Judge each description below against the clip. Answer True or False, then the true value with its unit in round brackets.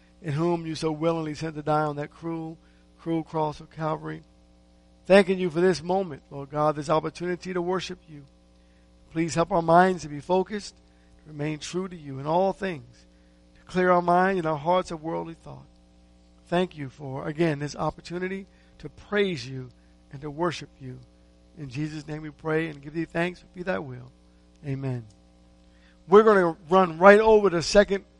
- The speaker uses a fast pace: False (185 wpm)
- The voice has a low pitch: False (155 Hz)